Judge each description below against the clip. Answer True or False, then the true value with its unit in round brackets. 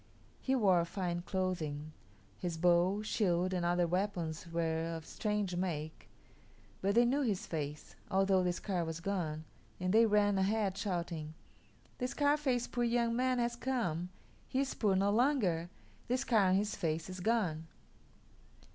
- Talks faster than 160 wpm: False (155 wpm)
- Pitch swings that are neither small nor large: True (4.7 semitones)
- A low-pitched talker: False (185 Hz)